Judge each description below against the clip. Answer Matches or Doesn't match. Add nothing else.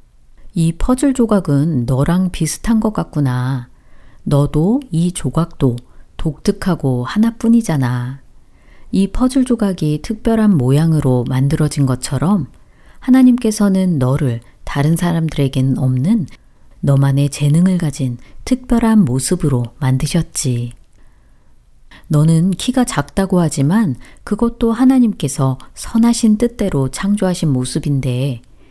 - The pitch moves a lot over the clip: Matches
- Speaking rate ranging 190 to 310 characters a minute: Matches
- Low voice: Doesn't match